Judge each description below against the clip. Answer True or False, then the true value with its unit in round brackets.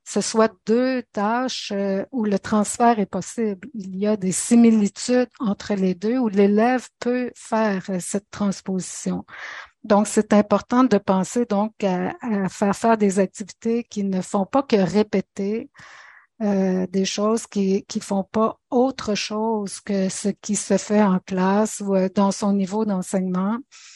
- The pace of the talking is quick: False (155 wpm)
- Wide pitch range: False (2.5 semitones)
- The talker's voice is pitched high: True (210 Hz)